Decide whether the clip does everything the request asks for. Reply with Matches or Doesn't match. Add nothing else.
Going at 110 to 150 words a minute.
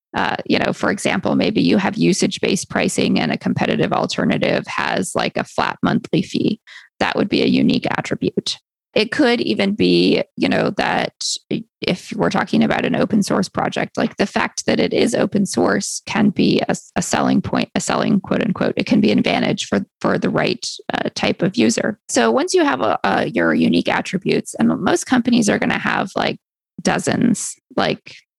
Doesn't match